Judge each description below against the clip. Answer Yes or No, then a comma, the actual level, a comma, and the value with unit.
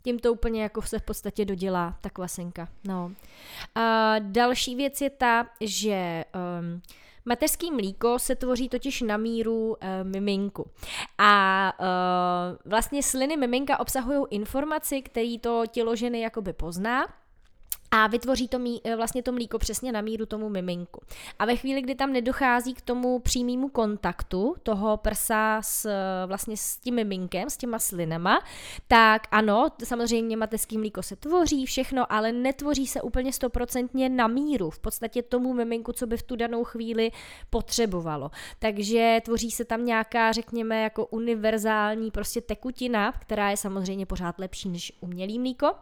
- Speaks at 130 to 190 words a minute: Yes, average, 150 wpm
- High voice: Yes, high, 225 Hz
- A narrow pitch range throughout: No, average, 3.3 semitones